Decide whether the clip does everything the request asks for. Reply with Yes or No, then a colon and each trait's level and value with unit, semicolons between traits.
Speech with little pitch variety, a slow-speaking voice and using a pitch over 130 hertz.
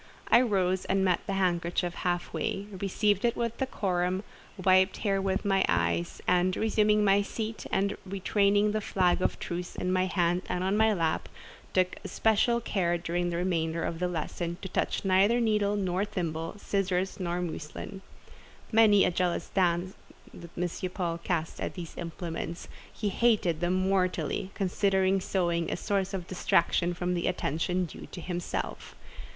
No: narrow, 2.3 semitones; average, 160 wpm; medium, 185 Hz